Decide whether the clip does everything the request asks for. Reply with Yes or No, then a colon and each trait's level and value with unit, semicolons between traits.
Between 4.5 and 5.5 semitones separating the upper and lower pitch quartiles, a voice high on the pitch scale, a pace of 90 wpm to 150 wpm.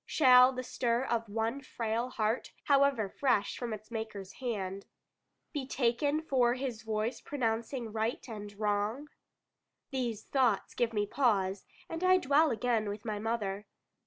No: average, 3.4 semitones; high, 230 Hz; average, 145 wpm